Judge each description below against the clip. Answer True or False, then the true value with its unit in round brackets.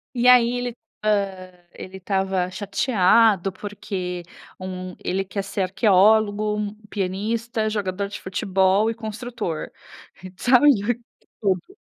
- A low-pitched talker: False (200 Hz)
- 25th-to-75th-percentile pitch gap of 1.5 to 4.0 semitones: True (2.7 semitones)